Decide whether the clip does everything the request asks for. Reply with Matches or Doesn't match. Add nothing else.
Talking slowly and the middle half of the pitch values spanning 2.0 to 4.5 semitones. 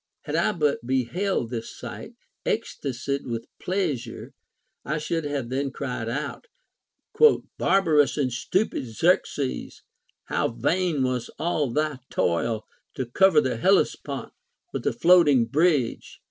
Doesn't match